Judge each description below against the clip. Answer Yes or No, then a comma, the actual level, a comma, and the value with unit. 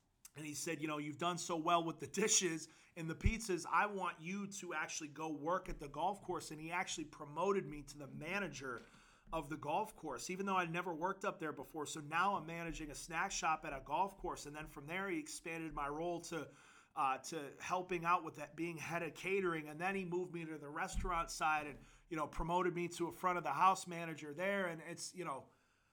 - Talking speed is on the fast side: Yes, fast, 235 wpm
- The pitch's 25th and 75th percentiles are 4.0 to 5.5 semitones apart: No, average, 2.8 semitones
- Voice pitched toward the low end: No, medium, 165 Hz